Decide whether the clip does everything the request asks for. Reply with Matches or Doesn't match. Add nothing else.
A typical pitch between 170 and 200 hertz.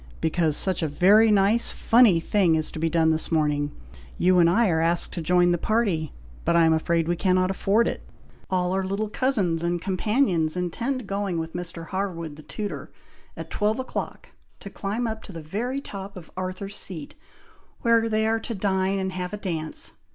Matches